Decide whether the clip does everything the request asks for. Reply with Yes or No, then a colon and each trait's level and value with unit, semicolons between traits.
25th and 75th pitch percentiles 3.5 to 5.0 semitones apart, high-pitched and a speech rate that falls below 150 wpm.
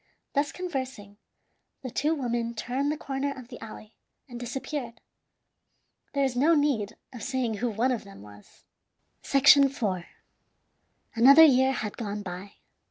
Yes: average, 4.1 semitones; very high, 250 Hz; average, 140 wpm